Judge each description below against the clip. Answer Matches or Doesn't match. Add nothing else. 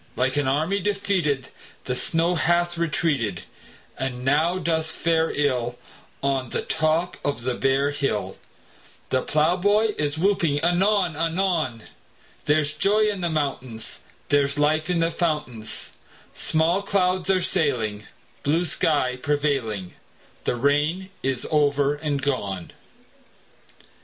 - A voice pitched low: Doesn't match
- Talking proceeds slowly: Matches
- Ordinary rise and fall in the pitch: Matches